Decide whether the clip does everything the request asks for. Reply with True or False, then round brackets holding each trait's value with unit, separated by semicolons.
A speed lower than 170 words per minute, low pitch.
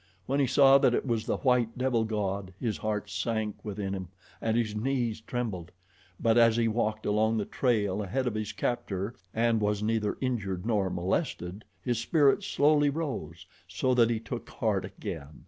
False (180 wpm; 110 Hz)